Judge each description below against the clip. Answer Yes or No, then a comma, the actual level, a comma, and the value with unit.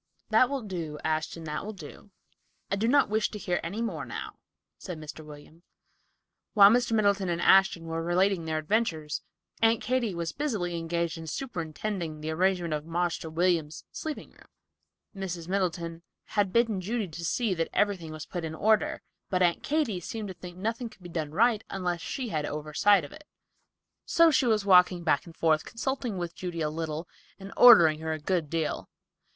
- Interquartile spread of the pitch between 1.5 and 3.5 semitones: No, average, 4.6 semitones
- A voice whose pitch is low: No, medium, 180 Hz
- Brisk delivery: No, average, 185 wpm